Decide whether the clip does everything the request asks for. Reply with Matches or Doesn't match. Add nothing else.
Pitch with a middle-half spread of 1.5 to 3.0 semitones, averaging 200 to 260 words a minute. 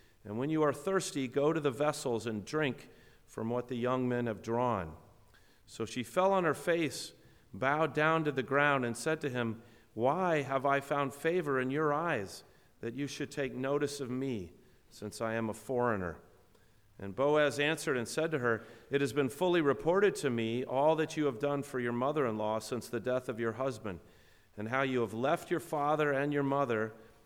Doesn't match